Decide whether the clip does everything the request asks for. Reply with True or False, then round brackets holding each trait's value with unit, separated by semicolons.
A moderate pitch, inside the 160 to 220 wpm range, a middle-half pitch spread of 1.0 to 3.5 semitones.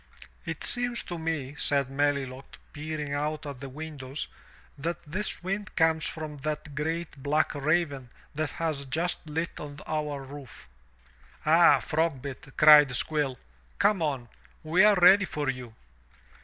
False (150 Hz; 140 wpm; 2.6 semitones)